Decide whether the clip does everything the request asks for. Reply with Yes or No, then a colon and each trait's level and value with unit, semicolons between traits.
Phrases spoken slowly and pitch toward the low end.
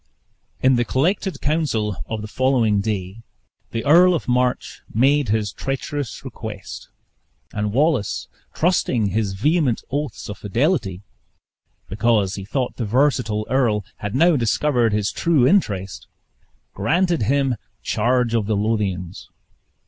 Yes: slow, 125 wpm; low, 120 Hz